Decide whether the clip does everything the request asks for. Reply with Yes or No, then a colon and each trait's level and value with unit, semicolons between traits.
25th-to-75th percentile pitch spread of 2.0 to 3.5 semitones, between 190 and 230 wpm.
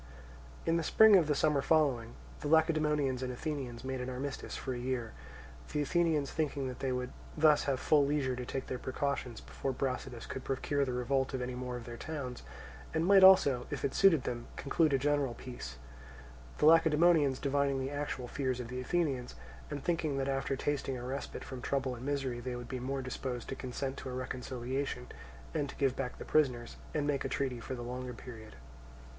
Yes: narrow, 2.6 semitones; fast, 205 wpm